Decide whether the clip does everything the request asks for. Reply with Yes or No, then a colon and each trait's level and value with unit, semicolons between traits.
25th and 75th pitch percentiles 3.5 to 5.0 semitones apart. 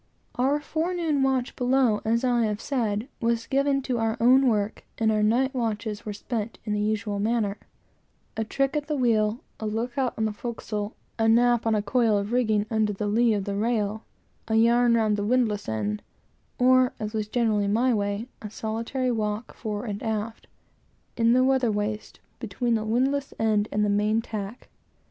No: average, 2.8 semitones